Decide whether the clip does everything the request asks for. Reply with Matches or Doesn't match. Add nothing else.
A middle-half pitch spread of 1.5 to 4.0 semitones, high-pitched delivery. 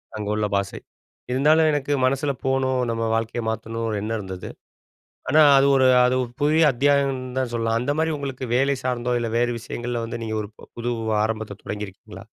Doesn't match